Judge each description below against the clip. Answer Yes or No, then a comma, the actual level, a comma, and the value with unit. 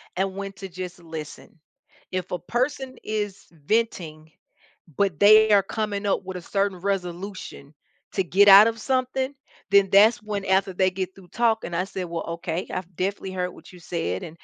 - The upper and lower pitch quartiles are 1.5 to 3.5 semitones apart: Yes, narrow, 2.6 semitones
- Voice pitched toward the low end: No, high, 190 Hz